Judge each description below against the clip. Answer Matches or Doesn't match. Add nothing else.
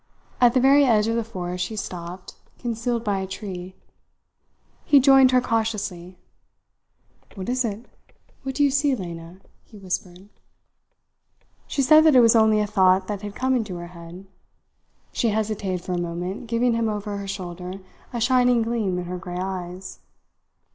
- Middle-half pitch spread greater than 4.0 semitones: Matches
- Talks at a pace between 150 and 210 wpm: Matches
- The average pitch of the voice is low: Doesn't match